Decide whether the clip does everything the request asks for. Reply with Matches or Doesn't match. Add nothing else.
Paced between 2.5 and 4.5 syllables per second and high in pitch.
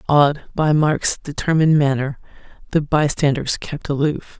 Doesn't match